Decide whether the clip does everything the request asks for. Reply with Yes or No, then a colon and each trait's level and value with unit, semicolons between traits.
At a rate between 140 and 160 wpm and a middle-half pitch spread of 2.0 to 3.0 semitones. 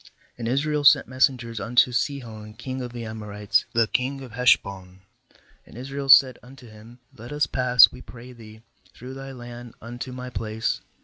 No: average, 170 wpm; narrow, 2.6 semitones